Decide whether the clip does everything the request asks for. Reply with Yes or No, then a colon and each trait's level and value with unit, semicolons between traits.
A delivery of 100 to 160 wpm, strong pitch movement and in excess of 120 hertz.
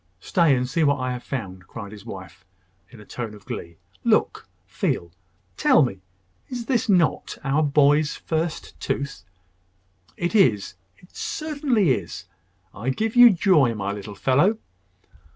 Yes: average, 150 wpm; wide, 8.6 semitones; low, 135 Hz